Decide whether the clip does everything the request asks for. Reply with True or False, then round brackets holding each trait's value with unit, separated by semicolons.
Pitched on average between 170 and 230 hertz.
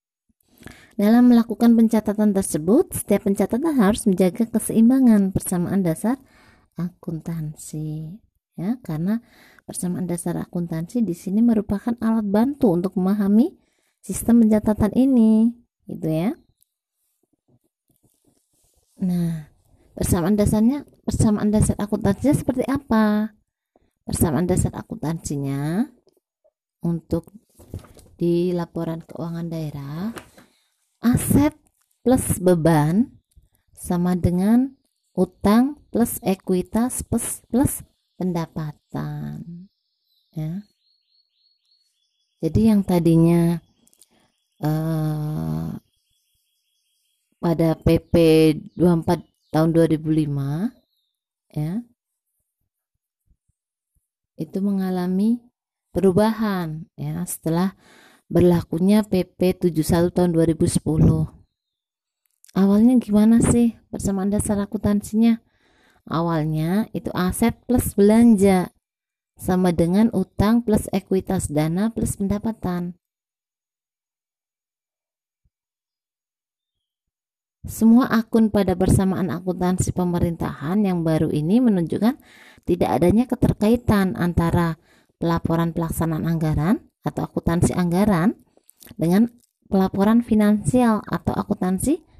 True (190 Hz)